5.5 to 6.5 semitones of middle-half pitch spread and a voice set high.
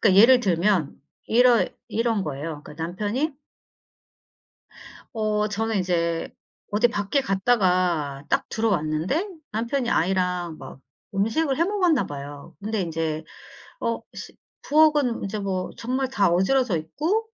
Yes: wide, 6.1 semitones; high, 205 Hz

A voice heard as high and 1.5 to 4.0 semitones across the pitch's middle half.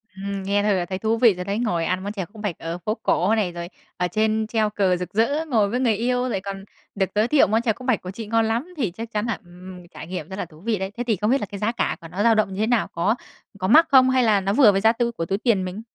Yes: high, 210 Hz; average, 3.5 semitones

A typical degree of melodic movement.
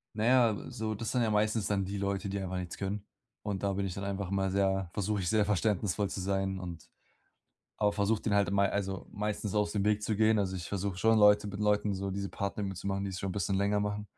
No: narrow, 1.3 semitones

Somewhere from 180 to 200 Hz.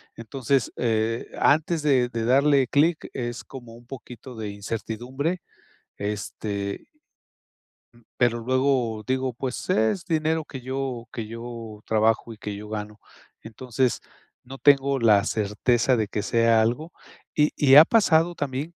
No: low, 120 Hz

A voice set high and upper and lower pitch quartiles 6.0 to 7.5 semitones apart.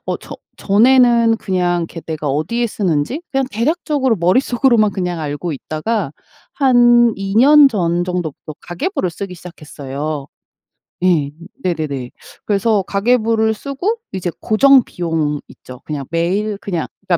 Yes: high, 195 Hz; wide, 6.3 semitones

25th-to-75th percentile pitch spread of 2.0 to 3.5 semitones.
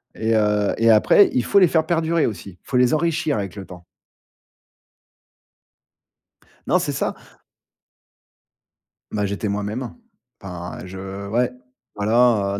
No: average, 4.1 semitones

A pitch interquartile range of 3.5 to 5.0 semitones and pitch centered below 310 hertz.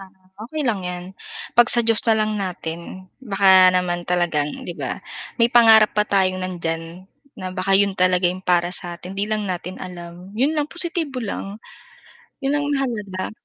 Yes: average, 4.0 semitones; high, 190 Hz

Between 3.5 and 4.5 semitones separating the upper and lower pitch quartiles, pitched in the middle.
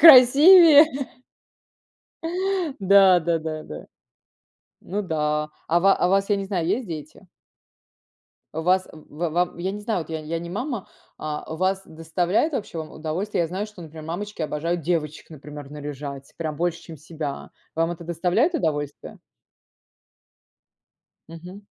Yes: average, 4.0 semitones; medium, 170 Hz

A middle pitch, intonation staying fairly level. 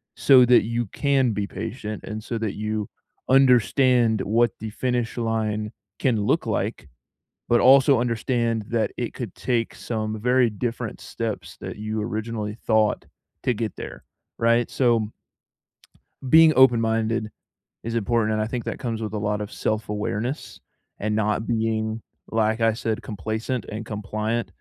No: low, 115 Hz; narrow, 1.9 semitones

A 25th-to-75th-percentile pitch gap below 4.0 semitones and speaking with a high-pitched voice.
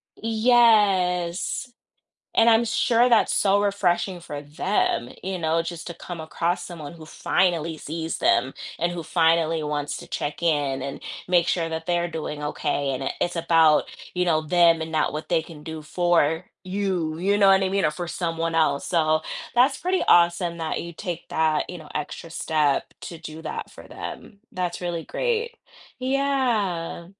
No: average, 3.0 semitones; medium, 170 Hz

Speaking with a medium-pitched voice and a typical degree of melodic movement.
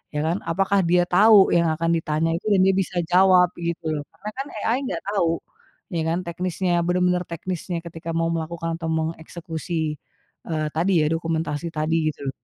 No: medium, 170 Hz; narrow, 1.9 semitones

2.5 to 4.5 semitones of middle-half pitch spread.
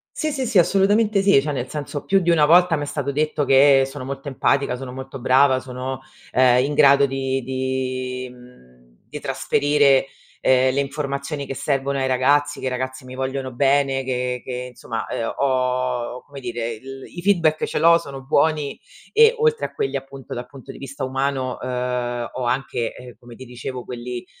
No: narrow, 2.1 semitones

